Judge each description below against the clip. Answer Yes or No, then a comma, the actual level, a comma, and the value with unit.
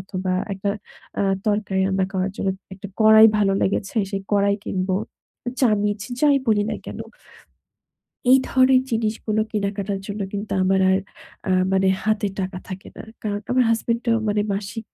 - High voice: Yes, high, 205 Hz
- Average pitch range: No, narrow, 2.0 semitones